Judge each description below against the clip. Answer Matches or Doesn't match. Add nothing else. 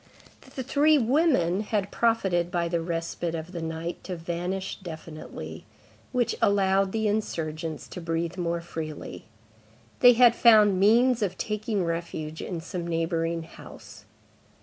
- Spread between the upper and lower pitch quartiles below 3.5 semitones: Doesn't match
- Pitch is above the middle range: Doesn't match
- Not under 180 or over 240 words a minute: Doesn't match